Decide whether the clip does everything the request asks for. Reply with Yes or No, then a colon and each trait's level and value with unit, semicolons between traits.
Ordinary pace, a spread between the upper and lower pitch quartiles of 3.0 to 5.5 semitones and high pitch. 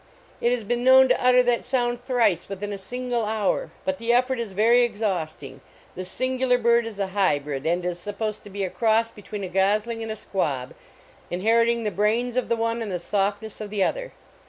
No: fast, 210 wpm; average, 3.7 semitones; high, 220 Hz